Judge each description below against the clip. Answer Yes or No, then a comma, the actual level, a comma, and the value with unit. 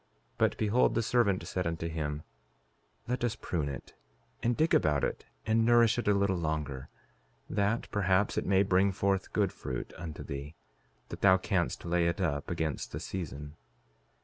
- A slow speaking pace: No, average, 175 wpm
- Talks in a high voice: No, very low, 95 Hz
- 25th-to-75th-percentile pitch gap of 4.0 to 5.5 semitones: Yes, average, 4.8 semitones